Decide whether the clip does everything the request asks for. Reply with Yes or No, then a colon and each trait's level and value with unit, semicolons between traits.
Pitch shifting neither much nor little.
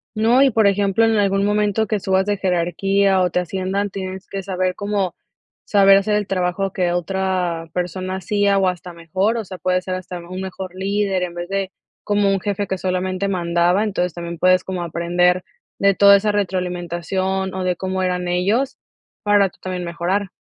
No: narrow, 1.8 semitones